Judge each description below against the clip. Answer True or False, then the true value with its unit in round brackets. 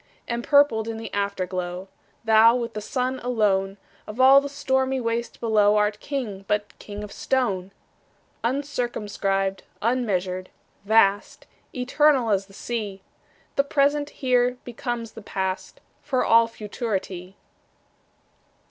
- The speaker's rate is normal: False (120 wpm)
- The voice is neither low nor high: False (225 Hz)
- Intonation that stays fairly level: False (4.1 semitones)